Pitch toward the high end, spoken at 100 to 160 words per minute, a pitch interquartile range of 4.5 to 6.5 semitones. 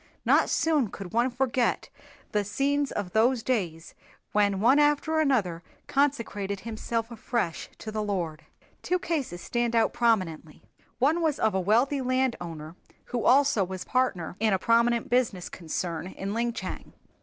Yes: high, 230 Hz; average, 150 wpm; average, 5.3 semitones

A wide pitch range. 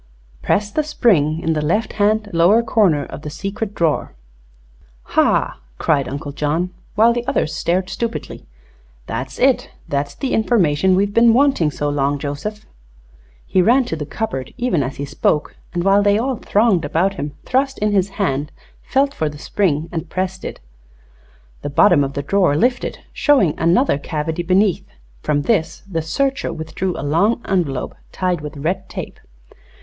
Yes: wide, 6.2 semitones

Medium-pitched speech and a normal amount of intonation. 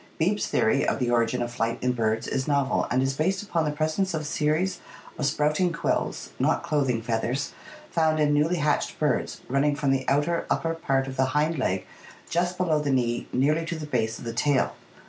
Yes: medium, 145 Hz; average, 3.7 semitones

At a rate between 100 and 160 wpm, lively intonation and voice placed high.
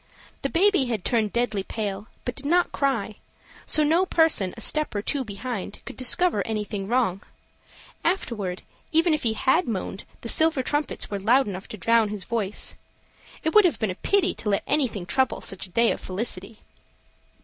No: average, 180 wpm; wide, 6.3 semitones; high, 230 Hz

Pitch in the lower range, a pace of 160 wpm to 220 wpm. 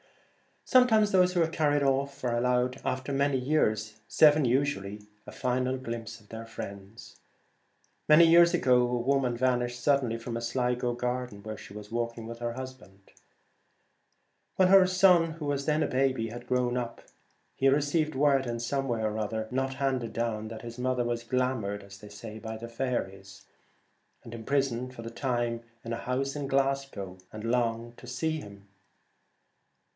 Yes: low, 125 Hz; average, 165 wpm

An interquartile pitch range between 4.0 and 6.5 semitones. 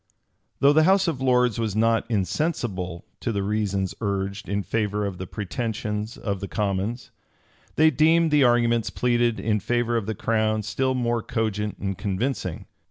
No: average, 3.4 semitones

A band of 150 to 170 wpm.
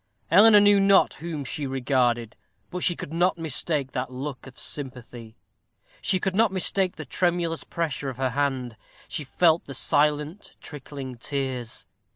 Yes: average, 155 wpm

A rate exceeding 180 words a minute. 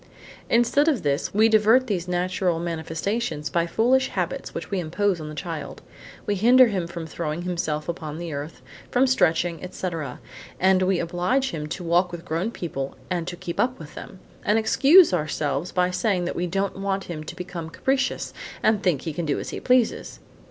Yes: average, 190 wpm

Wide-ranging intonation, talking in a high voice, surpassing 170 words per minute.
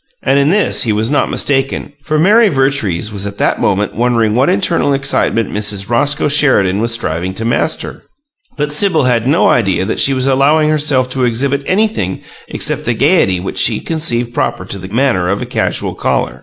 No: wide, 5.7 semitones; low, 125 Hz; average, 190 wpm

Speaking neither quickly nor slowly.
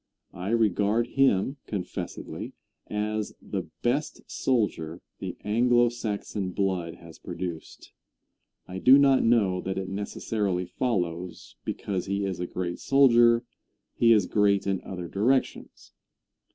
No: slow, 125 wpm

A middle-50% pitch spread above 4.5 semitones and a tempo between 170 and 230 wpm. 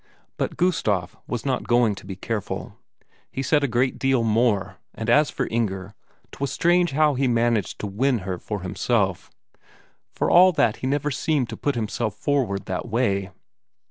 Yes: average, 5.1 semitones; average, 175 wpm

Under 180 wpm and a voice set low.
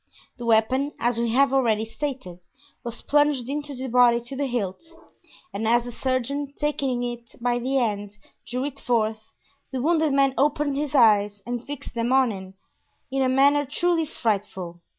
No: average, 170 wpm; very high, 250 Hz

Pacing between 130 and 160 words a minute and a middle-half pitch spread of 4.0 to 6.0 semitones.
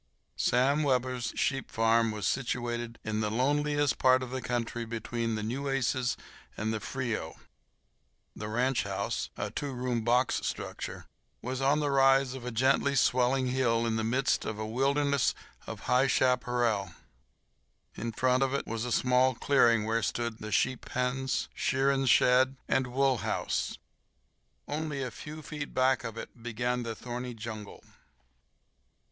No: average, 150 wpm; narrow, 2.6 semitones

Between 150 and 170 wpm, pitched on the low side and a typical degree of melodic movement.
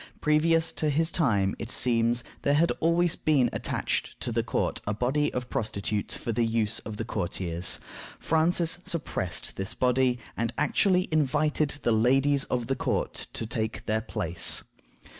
No: average, 160 wpm; low, 125 Hz; wide, 5.7 semitones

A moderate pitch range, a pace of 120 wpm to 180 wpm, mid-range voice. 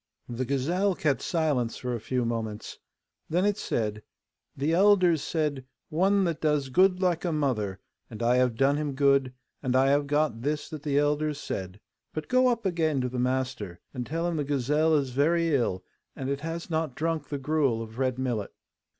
No: average, 4.2 semitones; average, 195 wpm; medium, 145 Hz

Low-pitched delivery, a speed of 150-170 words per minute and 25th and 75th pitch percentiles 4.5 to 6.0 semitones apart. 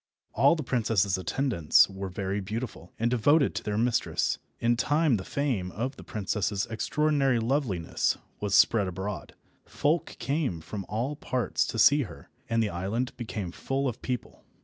Yes: low, 115 Hz; average, 160 wpm; wide, 5.4 semitones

